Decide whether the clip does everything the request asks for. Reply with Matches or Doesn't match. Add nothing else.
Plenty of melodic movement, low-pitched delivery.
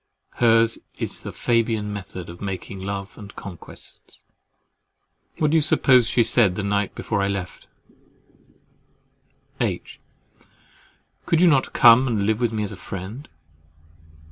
Doesn't match